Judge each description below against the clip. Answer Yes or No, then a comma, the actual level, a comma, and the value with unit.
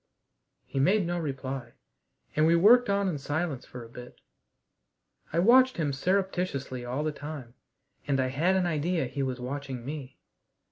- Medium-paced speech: Yes, average, 160 wpm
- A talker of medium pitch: Yes, medium, 145 Hz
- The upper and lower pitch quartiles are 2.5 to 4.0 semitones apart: No, average, 5.1 semitones